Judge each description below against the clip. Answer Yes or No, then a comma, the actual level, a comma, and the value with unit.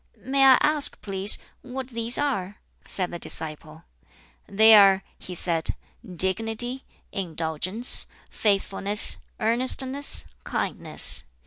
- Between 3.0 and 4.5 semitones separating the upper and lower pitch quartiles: No, average, 5.1 semitones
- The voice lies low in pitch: No, high, 210 Hz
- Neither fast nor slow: No, slow, 100 wpm